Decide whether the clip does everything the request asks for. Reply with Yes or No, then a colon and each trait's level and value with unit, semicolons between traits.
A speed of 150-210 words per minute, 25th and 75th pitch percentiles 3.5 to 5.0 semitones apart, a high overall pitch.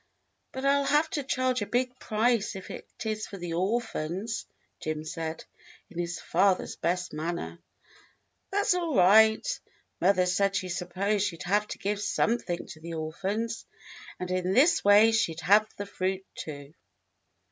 Yes: average, 160 wpm; average, 4.3 semitones; high, 200 Hz